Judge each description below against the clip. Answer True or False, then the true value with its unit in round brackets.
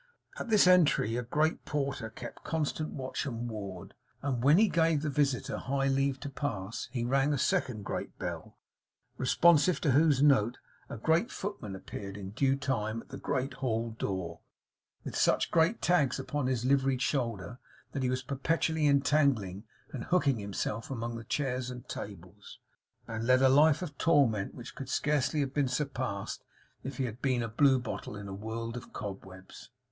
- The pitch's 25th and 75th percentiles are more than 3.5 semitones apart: True (4.0 semitones)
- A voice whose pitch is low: True (130 Hz)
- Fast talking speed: False (175 wpm)